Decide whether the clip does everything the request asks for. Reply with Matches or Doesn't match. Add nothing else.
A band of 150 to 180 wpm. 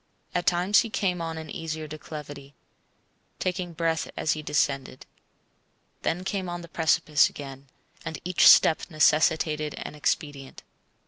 Doesn't match